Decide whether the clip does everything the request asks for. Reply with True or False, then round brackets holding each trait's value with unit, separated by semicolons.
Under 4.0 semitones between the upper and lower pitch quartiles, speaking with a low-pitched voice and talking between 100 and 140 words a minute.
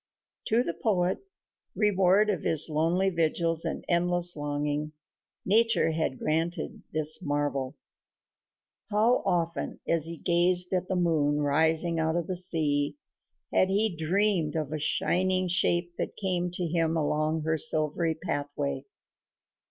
False (2.9 semitones; 165 Hz; 135 wpm)